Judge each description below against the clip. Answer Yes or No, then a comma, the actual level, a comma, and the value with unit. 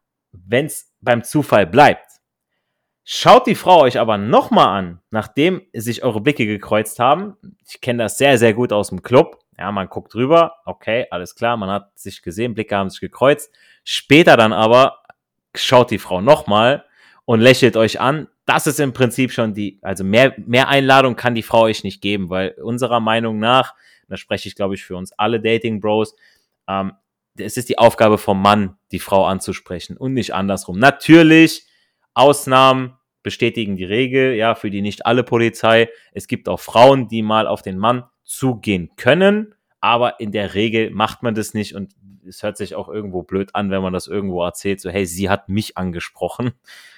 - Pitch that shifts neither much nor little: Yes, average, 4.2 semitones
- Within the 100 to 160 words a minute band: No, average, 185 wpm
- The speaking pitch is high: No, low, 110 Hz